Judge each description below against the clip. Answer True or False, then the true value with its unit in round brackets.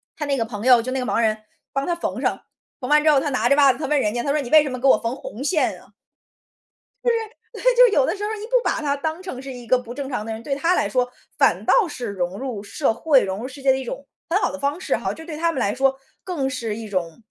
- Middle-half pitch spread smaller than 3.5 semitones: False (4.2 semitones)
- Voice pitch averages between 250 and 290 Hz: True (270 Hz)